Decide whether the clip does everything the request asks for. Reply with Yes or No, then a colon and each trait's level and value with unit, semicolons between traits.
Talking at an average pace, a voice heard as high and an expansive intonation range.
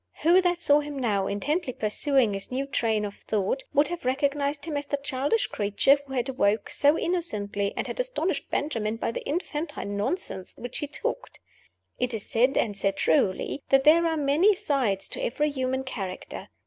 Yes: average, 185 wpm; very high, 270 Hz; wide, 5.8 semitones